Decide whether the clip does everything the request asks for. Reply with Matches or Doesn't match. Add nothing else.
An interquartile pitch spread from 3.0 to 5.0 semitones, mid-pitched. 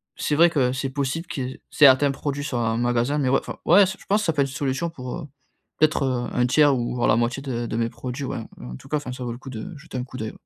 Doesn't match